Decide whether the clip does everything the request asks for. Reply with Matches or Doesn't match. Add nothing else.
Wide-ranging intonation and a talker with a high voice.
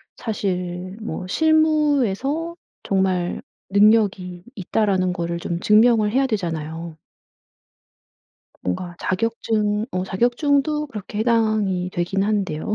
Doesn't match